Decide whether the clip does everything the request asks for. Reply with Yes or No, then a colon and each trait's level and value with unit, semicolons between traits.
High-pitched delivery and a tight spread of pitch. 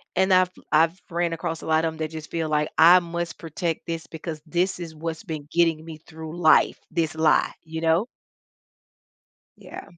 No: medium, 165 Hz; narrow, 1.4 semitones